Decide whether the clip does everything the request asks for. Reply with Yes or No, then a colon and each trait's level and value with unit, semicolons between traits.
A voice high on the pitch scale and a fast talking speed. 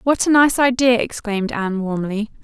No: high, 230 Hz; average, 170 wpm